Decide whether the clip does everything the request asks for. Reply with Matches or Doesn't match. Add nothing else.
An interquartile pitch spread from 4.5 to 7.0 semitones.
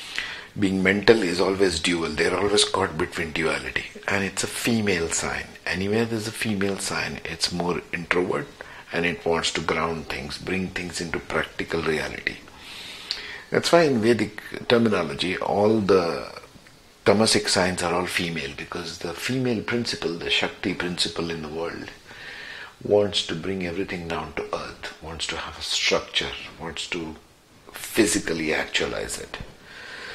Doesn't match